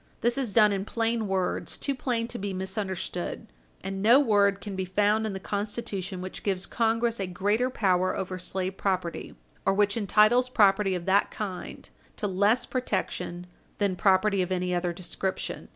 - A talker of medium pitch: No, high, 200 Hz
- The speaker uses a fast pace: No, average, 170 wpm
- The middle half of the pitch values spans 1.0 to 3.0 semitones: Yes, average, 2.7 semitones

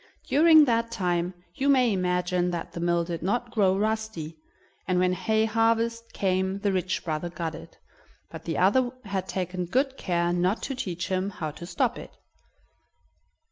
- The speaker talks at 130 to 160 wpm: No, average, 170 wpm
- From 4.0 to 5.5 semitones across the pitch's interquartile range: Yes, average, 4.5 semitones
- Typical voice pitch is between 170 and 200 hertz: Yes, high, 190 Hz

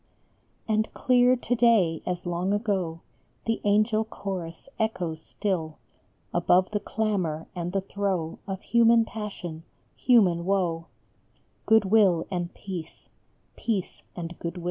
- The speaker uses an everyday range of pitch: Yes, average, 4.1 semitones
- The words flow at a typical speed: No, slow, 125 wpm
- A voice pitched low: No, high, 190 Hz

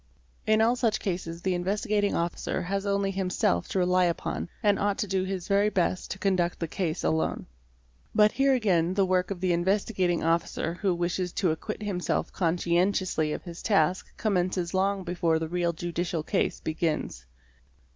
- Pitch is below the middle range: No, medium, 185 Hz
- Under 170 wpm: No, average, 175 wpm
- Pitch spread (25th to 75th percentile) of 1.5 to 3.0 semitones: Yes, narrow, 2.5 semitones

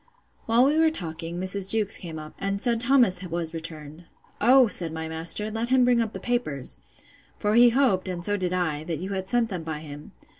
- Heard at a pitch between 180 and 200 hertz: Yes, high, 190 Hz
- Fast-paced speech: Yes, fast, 215 wpm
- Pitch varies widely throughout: Yes, wide, 6.0 semitones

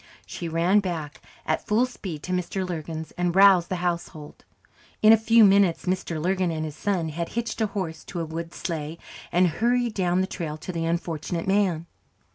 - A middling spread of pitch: Yes, average, 3.1 semitones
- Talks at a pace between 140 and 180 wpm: No, average, 190 wpm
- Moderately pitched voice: Yes, medium, 175 Hz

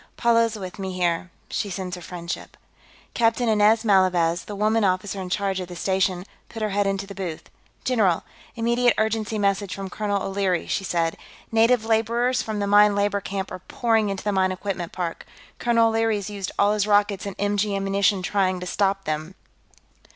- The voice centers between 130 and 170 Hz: No, high, 200 Hz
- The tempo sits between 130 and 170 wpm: No, average, 185 wpm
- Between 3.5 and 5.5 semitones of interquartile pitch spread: No, narrow, 2.5 semitones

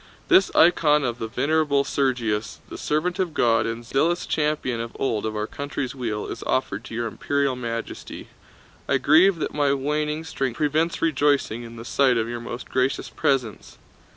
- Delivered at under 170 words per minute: No, average, 175 wpm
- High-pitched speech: No, low, 135 Hz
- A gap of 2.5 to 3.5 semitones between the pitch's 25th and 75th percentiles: No, average, 4.3 semitones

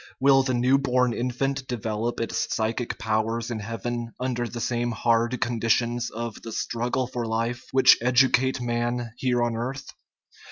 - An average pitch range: No, narrow, 1.5 semitones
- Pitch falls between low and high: No, low, 120 Hz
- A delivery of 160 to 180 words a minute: Yes, average, 165 wpm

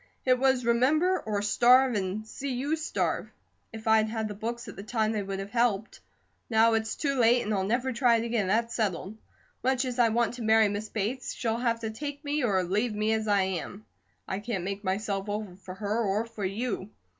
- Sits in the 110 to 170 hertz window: No, high, 220 Hz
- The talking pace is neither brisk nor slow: No, fast, 215 wpm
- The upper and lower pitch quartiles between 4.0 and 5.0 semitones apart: No, average, 3.0 semitones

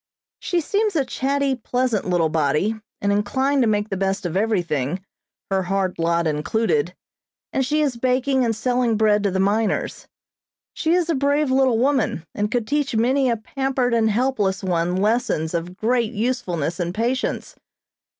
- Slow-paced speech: No, average, 165 wpm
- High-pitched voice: Yes, high, 225 Hz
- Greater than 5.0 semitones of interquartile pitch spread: Yes, wide, 5.5 semitones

